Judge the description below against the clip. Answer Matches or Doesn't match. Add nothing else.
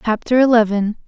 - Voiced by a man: Doesn't match